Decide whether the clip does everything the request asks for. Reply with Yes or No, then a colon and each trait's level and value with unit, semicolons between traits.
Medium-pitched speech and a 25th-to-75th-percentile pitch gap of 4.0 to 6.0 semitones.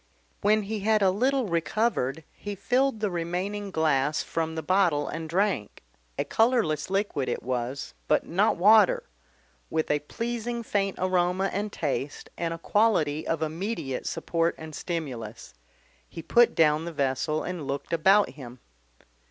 Yes: medium, 170 Hz; average, 5.2 semitones